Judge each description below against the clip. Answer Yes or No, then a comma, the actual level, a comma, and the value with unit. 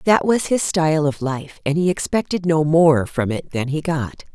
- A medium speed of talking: No, fast, 220 wpm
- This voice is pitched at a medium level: Yes, medium, 160 Hz